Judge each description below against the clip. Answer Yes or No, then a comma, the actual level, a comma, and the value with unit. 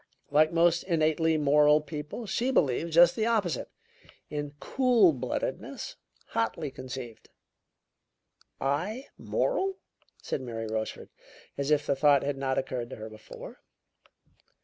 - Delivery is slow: Yes, slow, 125 wpm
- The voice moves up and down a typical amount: Yes, average, 4.5 semitones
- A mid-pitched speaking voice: Yes, medium, 150 Hz